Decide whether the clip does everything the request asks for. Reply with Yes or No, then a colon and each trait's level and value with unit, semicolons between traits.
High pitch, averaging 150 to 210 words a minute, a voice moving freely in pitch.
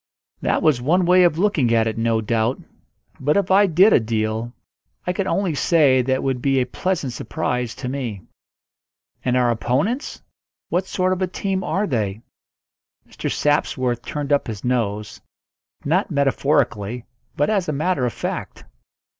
No: low, 135 Hz; average, 165 wpm; wide, 7.0 semitones